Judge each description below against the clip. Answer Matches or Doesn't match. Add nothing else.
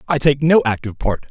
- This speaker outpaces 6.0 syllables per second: Matches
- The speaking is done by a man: Matches